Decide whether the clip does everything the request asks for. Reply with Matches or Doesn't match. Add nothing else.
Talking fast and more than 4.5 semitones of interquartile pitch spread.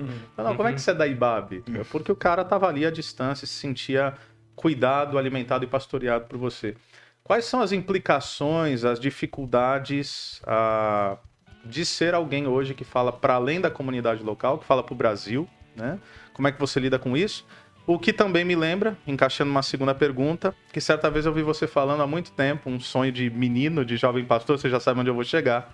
Doesn't match